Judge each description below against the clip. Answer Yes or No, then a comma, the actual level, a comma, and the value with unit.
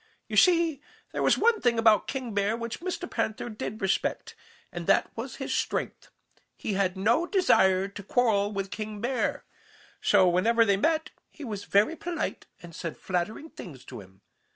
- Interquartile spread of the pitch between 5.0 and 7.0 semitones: Yes, wide, 5.4 semitones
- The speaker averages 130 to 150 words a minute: No, average, 175 wpm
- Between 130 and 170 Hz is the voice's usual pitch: No, high, 215 Hz